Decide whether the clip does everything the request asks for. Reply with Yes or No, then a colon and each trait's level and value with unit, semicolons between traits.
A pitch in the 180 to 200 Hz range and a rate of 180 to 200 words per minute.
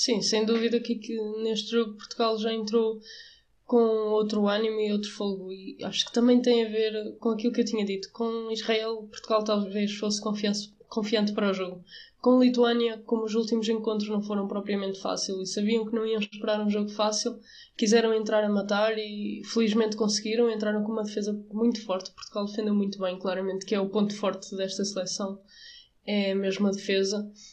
No: high, 215 Hz; fast, 185 wpm